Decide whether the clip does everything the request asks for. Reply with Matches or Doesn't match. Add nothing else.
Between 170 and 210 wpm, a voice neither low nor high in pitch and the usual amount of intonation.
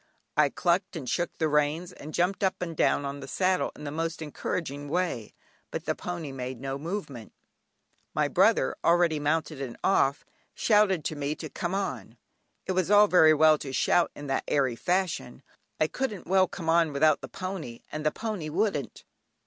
Matches